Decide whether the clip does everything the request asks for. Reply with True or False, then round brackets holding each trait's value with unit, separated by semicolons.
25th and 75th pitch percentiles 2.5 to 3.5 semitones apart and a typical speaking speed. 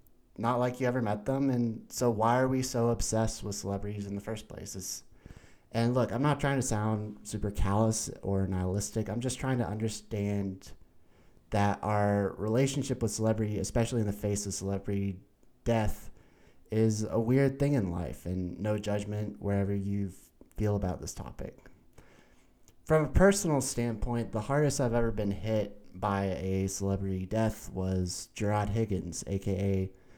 True (3.1 semitones; 160 wpm)